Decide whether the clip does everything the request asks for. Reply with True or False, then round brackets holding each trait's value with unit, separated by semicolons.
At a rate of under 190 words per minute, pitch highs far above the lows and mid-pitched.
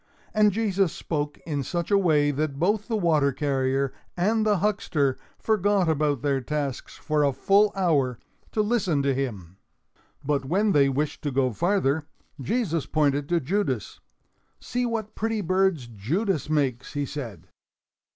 True (150 wpm; 6.3 semitones; 155 Hz)